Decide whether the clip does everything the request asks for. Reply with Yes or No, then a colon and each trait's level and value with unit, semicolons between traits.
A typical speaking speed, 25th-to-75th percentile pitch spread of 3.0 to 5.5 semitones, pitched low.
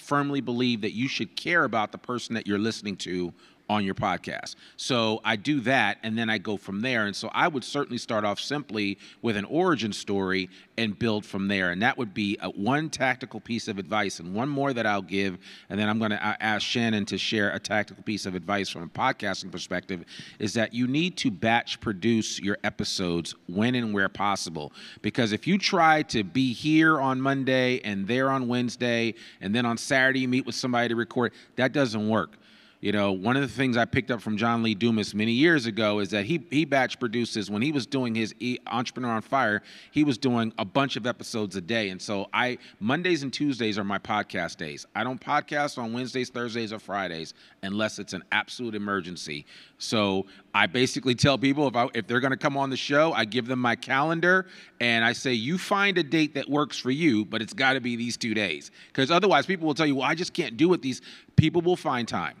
No: fast, 225 wpm; average, 4.1 semitones; low, 115 Hz